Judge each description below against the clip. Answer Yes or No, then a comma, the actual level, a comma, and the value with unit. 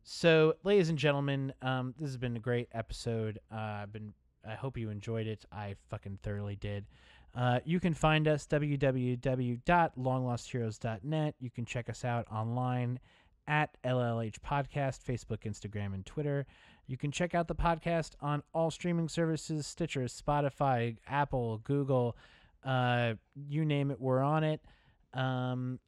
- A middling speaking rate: Yes, average, 145 wpm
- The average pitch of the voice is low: Yes, low, 130 Hz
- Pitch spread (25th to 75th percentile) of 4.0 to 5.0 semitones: Yes, average, 4.5 semitones